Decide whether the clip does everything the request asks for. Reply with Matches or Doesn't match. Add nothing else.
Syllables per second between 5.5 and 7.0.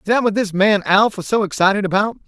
Matches